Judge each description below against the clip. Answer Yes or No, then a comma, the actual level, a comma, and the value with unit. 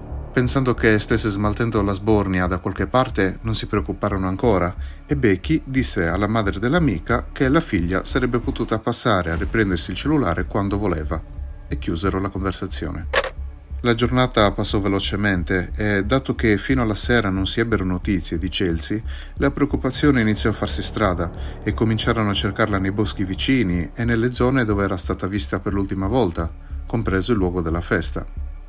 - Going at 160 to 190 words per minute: Yes, average, 165 wpm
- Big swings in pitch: No, average, 4.4 semitones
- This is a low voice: Yes, low, 100 Hz